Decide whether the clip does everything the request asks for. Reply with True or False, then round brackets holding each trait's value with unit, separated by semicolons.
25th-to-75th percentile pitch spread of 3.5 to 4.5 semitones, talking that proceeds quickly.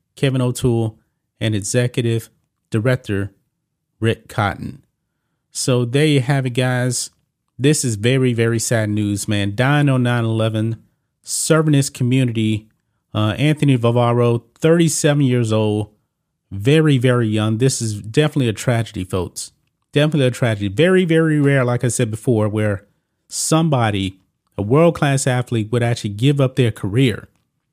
False (4.2 semitones; 135 wpm)